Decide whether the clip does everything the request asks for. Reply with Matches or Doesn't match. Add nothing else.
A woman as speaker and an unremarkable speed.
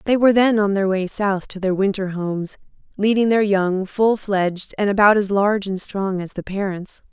Doesn't match